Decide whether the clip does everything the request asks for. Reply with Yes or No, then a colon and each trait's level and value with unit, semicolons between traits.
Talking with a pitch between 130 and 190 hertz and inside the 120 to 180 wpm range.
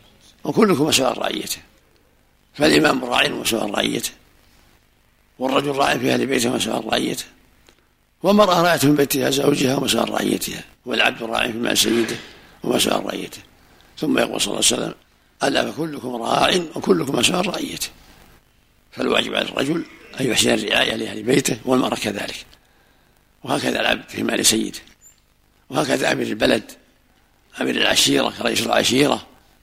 Yes: low, 135 Hz; average, 130 wpm